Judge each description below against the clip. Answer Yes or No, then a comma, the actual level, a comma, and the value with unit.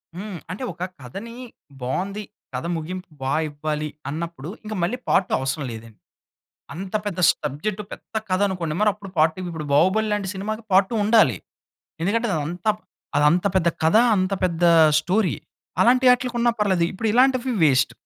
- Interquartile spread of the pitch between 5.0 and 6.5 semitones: Yes, average, 5.3 semitones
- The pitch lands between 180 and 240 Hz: Yes, medium, 185 Hz